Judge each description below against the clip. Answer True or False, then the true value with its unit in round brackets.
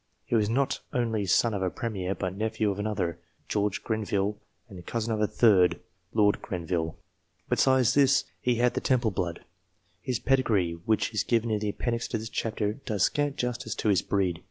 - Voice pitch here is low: True (110 Hz)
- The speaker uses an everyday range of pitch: True (3.3 semitones)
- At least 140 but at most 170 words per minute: False (185 wpm)